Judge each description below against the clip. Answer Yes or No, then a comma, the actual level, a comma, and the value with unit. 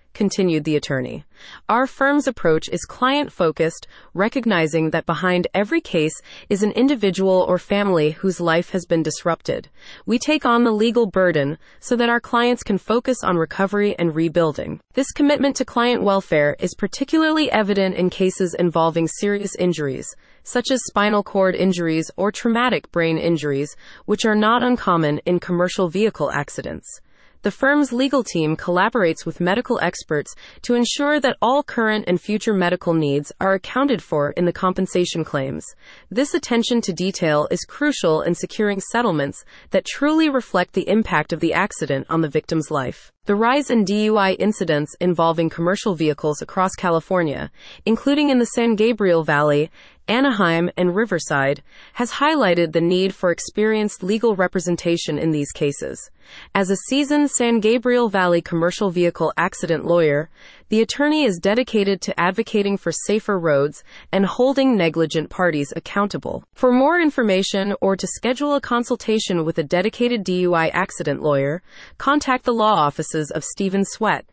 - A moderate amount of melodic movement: No, wide, 5.9 semitones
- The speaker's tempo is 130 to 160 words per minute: Yes, average, 155 wpm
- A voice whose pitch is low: No, high, 190 Hz